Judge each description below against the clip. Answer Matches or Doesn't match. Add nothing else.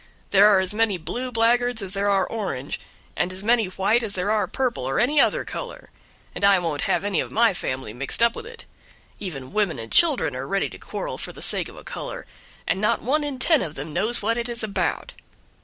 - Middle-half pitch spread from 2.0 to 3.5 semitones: Doesn't match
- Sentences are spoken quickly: Matches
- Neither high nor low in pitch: Doesn't match